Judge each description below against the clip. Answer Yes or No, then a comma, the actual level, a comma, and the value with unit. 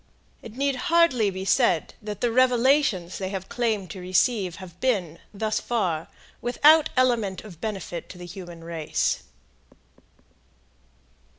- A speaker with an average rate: No, slow, 130 wpm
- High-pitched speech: Yes, high, 205 Hz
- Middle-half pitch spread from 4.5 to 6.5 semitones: Yes, wide, 5.4 semitones